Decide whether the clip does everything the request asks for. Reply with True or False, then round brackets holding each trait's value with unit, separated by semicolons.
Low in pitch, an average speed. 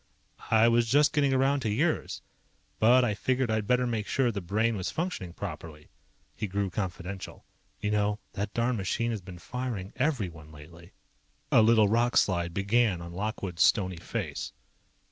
True (105 Hz; 160 wpm)